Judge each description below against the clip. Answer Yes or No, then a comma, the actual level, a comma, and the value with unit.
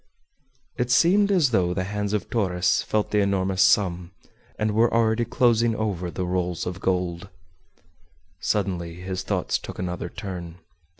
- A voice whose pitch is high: No, very low, 95 Hz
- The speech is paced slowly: No, average, 145 wpm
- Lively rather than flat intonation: No, average, 3.4 semitones